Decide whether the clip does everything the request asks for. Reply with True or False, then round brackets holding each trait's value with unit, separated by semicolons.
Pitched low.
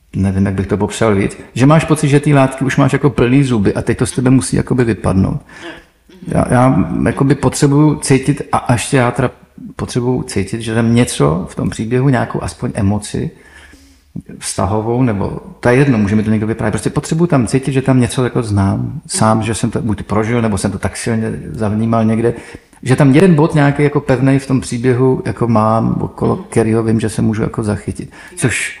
True (120 Hz)